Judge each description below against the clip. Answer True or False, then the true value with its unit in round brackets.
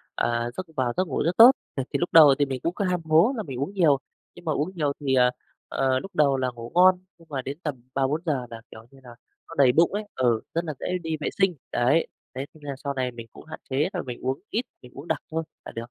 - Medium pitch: True (145 Hz)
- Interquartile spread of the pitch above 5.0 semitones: False (4.5 semitones)